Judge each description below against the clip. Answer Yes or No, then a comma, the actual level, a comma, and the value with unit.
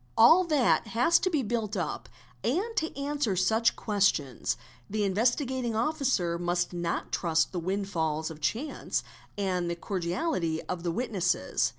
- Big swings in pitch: Yes, wide, 6.6 semitones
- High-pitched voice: Yes, high, 200 Hz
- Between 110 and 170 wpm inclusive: Yes, average, 160 wpm